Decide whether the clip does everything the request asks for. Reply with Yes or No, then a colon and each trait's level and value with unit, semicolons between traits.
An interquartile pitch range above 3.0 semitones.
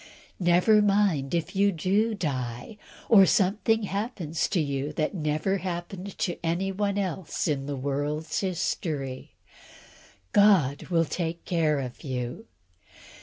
Yes: average, 5.1 semitones